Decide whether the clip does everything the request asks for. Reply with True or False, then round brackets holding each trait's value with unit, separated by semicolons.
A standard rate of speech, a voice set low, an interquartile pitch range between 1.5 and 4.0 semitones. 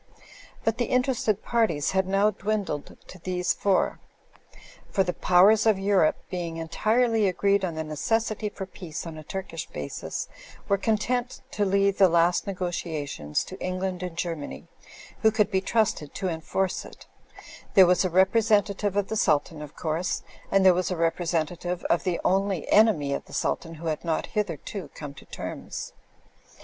False (165 wpm; 185 Hz; 3.6 semitones)